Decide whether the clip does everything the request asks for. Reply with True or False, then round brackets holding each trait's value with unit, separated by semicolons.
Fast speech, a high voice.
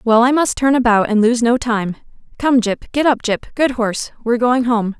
True (230 wpm; 240 Hz)